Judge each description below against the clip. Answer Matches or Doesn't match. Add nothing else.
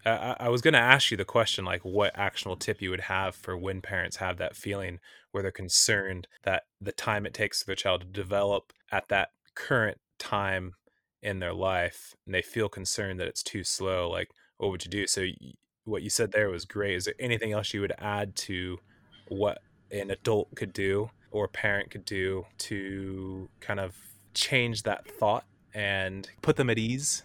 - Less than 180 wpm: Doesn't match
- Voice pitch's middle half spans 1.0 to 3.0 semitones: Matches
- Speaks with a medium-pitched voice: Doesn't match